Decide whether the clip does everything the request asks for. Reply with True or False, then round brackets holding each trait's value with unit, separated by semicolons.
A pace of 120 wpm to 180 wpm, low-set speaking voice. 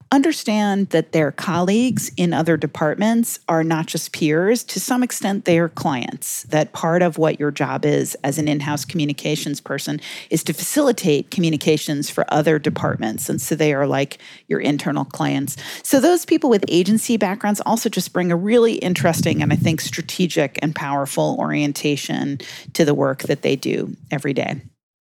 False (175 wpm; 160 Hz)